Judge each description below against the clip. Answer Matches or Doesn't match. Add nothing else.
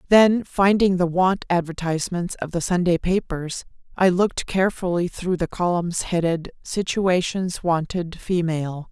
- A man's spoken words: Doesn't match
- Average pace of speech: Doesn't match